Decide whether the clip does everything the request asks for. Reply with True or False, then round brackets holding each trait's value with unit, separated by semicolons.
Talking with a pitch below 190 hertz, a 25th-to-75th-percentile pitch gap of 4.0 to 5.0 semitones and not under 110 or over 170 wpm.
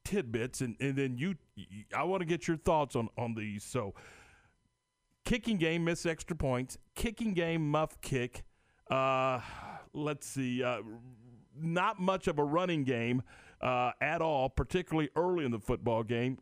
False (135 Hz; 5.5 semitones; 155 wpm)